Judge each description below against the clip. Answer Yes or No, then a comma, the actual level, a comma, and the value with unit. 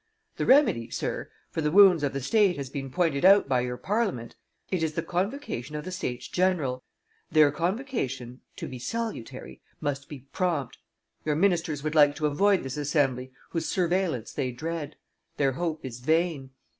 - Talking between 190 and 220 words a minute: No, average, 170 wpm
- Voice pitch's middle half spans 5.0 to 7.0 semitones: Yes, average, 5.3 semitones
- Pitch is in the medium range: Yes, medium, 150 Hz